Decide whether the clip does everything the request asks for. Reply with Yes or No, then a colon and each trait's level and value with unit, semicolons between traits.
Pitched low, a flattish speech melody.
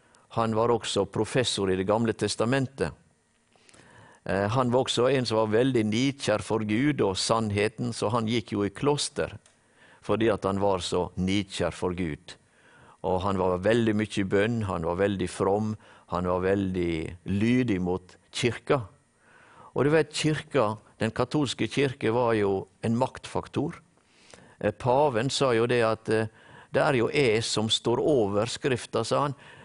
No: low, 110 Hz; average, 3.3 semitones